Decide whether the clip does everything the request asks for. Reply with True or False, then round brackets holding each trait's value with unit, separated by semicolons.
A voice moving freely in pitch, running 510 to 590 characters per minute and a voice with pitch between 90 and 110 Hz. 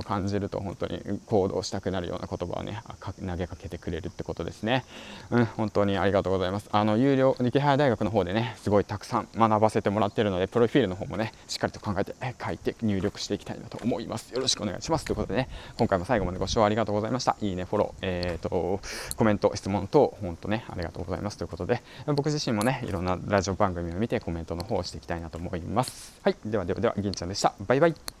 False (4.3 semitones; 530 characters per minute; 100 Hz)